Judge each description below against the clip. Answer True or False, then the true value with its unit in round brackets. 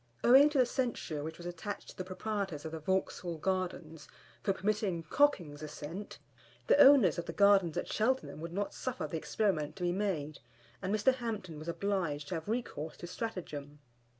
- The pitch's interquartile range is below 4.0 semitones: False (4.9 semitones)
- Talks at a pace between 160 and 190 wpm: True (180 wpm)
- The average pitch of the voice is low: False (185 Hz)